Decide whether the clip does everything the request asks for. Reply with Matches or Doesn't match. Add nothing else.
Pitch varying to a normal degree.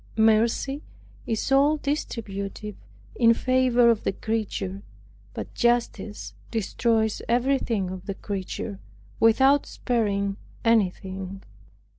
Matches